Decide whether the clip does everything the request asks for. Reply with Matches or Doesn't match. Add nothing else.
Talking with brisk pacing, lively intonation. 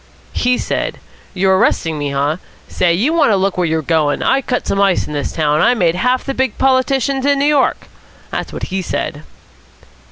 Matches